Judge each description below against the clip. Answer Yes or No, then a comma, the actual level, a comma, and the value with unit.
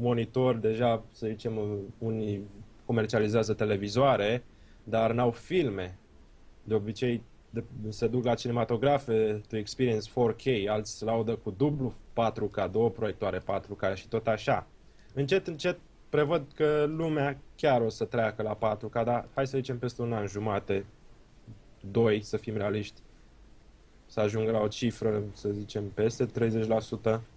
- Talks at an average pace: Yes, average, 140 wpm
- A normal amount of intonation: No, narrow, 2.2 semitones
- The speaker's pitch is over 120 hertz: No, low, 115 Hz